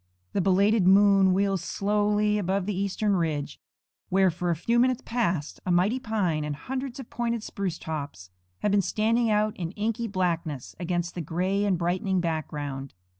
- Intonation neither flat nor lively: Yes, average, 3.6 semitones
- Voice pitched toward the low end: No, high, 190 Hz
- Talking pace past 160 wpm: Yes, average, 170 wpm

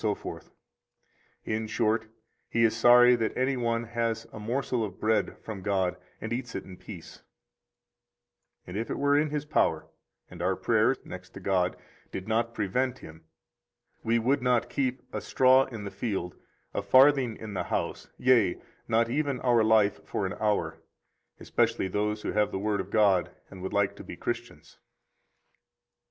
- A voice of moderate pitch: No, low, 110 Hz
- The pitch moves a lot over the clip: No, average, 3.6 semitones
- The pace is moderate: Yes, average, 170 wpm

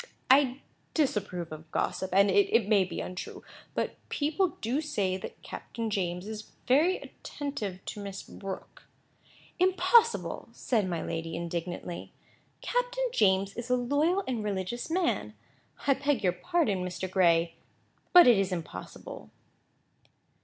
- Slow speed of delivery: Yes, slow, 130 wpm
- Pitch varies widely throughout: Yes, wide, 8.0 semitones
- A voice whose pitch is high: Yes, high, 210 Hz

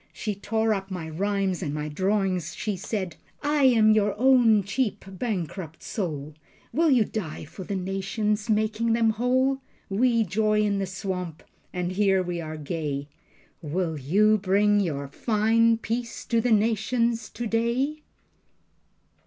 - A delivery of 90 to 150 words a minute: Yes, average, 145 wpm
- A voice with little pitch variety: No, average, 3.8 semitones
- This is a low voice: No, high, 205 Hz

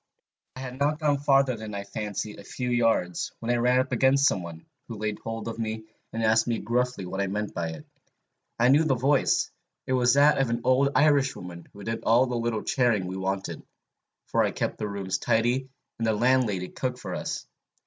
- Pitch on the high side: No, low, 115 Hz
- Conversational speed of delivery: No, fast, 210 wpm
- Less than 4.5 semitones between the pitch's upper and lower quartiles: Yes, average, 3.8 semitones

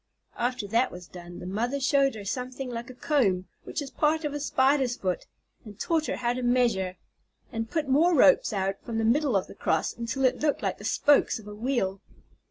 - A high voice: Yes, high, 245 Hz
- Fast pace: Yes, fast, 215 wpm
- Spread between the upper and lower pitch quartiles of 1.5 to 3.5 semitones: No, average, 5.1 semitones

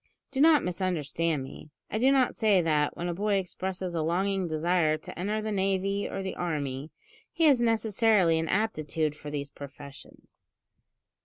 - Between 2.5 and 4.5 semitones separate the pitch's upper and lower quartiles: No, average, 5.1 semitones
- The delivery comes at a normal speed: Yes, average, 165 wpm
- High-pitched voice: No, medium, 180 Hz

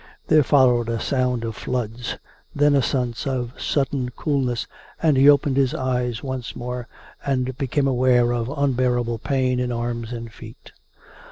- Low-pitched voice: Yes, low, 125 Hz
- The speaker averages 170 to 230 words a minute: No, average, 155 wpm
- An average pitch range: No, narrow, 2.1 semitones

